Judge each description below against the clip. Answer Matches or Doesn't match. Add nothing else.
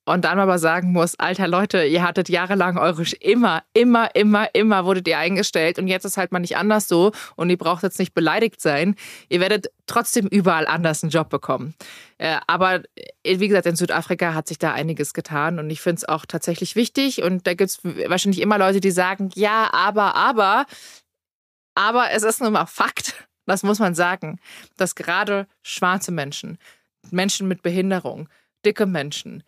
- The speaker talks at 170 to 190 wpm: Matches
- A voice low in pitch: Doesn't match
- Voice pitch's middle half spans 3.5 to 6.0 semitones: Doesn't match